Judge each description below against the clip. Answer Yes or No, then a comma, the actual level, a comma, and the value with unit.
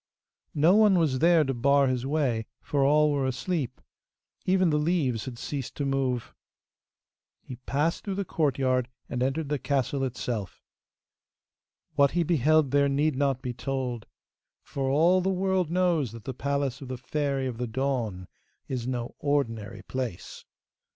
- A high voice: No, medium, 140 Hz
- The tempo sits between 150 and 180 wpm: Yes, average, 160 wpm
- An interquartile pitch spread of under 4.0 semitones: Yes, average, 3.2 semitones